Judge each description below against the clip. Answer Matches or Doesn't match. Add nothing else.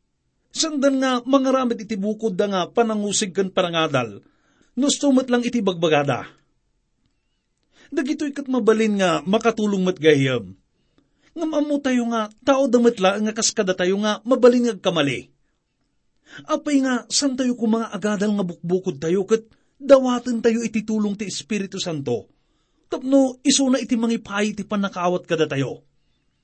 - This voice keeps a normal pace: Doesn't match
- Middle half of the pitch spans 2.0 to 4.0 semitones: Doesn't match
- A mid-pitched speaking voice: Doesn't match